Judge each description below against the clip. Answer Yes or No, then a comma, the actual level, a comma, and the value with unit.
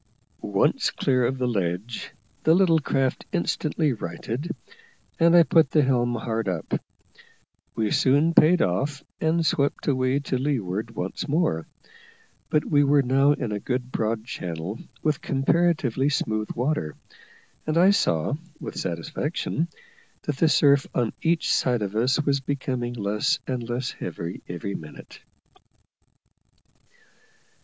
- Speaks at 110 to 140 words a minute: Yes, slow, 135 wpm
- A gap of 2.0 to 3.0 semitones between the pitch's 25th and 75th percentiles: No, wide, 5.5 semitones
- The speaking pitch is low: Yes, low, 130 Hz